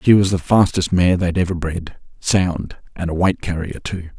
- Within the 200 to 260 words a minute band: No, average, 185 wpm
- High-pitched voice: No, very low, 90 Hz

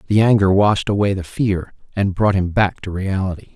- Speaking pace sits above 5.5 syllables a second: No, 5.0 syllables/s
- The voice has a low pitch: Yes, low, 100 Hz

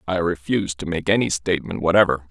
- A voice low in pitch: Yes, very low, 90 Hz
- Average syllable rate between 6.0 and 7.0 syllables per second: Yes, 6.5 syllables/s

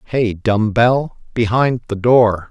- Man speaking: Yes, male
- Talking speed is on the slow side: Yes, slow, 95 wpm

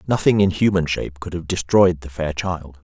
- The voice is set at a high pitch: No, very low, 85 Hz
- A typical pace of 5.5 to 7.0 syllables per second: No, 5.2 syllables/s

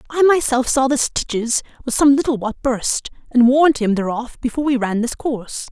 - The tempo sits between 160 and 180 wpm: No, average, 200 wpm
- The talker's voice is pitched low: No, very high, 255 Hz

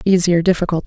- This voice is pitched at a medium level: Yes, medium, 175 Hz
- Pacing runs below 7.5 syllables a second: No, 8.0 syllables/s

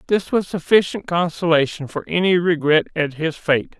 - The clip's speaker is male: Yes, male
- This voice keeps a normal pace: Yes, average, 160 wpm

